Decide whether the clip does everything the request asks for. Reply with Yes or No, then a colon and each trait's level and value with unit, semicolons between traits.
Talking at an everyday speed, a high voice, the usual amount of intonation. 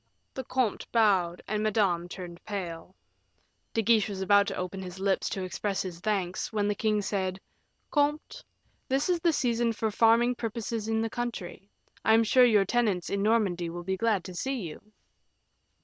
Yes: average, 180 wpm; high, 210 Hz; average, 3.5 semitones